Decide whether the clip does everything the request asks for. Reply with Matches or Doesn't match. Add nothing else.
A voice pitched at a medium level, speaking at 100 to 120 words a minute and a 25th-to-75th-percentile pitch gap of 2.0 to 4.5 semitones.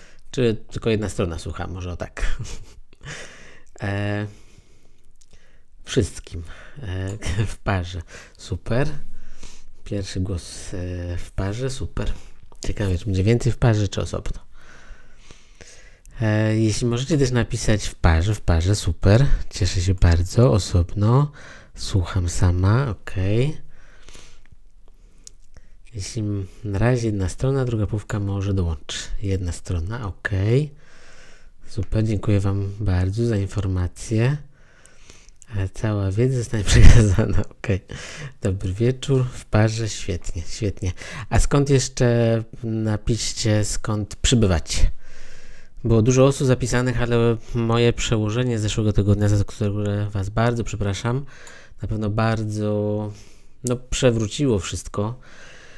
Doesn't match